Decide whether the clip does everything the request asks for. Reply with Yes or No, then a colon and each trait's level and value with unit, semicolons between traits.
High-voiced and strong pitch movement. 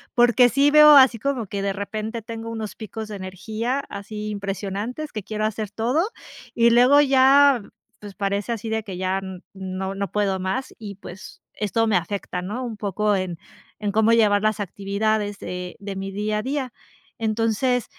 No: high, 215 Hz; average, 2.9 semitones